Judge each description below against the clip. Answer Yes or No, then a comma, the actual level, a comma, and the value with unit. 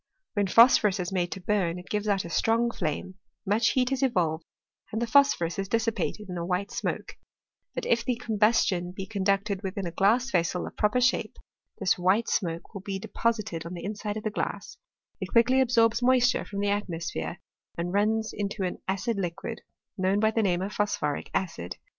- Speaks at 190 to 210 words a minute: Yes, average, 200 wpm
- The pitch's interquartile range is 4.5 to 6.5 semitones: No, average, 3.9 semitones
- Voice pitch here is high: Yes, high, 200 Hz